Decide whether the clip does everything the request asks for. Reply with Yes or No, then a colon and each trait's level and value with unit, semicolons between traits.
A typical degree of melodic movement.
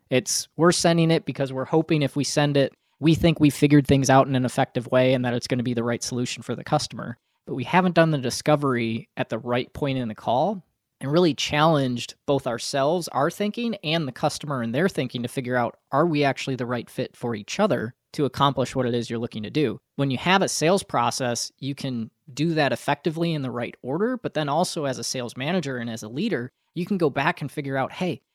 Yes: average, 4.3 semitones